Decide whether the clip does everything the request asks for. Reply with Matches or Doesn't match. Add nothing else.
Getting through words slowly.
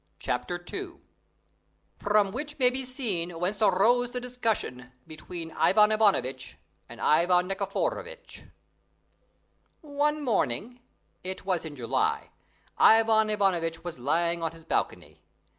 Matches